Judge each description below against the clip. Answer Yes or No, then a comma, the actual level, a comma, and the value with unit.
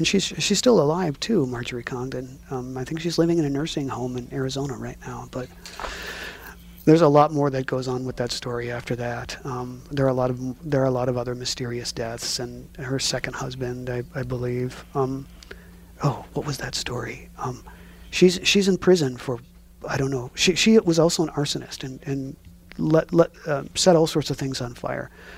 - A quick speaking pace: Yes, fast, 210 wpm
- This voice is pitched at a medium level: No, low, 130 Hz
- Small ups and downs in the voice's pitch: No, average, 3.8 semitones